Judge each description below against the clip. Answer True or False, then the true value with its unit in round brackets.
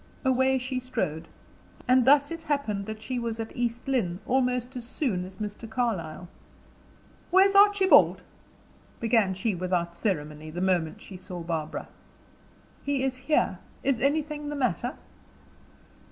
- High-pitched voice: True (235 Hz)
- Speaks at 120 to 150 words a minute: True (140 wpm)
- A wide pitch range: True (6.3 semitones)